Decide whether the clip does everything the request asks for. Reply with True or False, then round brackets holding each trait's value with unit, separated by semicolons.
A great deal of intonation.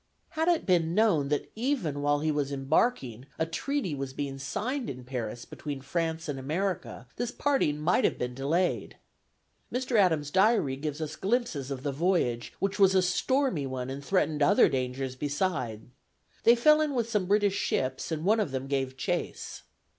True (6.9 semitones)